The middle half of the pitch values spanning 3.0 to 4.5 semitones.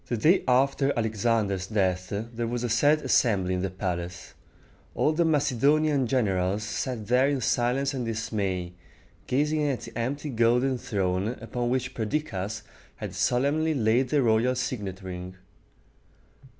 No: average, 5.0 semitones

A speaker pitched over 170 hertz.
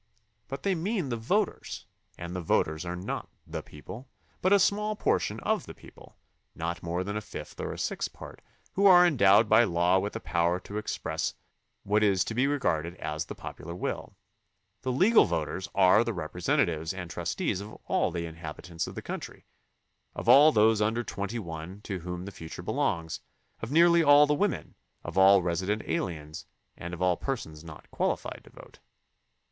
No: very low, 95 Hz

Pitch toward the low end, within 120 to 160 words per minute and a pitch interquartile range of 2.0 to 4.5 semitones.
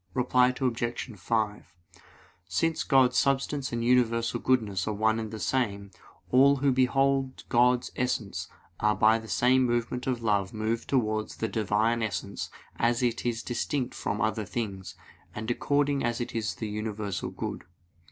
Yes: low, 115 Hz; average, 150 wpm; average, 2.8 semitones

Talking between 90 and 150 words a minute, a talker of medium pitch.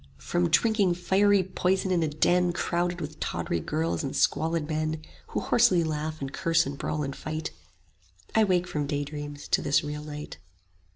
No: average, 170 wpm; medium, 155 Hz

